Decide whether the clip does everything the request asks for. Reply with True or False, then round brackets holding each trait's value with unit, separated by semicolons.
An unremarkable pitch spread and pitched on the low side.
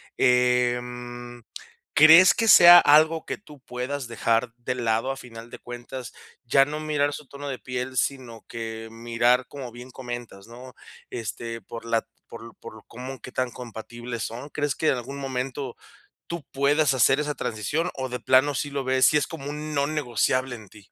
True (3.1 semitones; 125 Hz)